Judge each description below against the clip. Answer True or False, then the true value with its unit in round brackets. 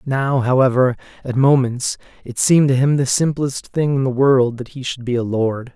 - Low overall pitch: True (130 Hz)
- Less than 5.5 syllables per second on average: True (4.9 syllables/s)